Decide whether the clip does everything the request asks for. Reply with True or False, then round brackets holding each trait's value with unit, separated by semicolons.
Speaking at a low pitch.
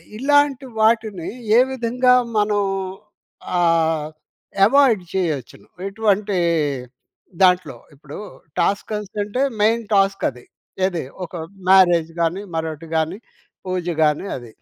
False (190 Hz)